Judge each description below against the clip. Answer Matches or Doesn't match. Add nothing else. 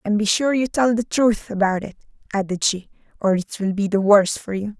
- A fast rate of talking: Matches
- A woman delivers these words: Matches